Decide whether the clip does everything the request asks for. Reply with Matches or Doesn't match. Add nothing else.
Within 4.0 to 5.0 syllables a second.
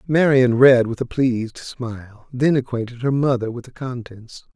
Matches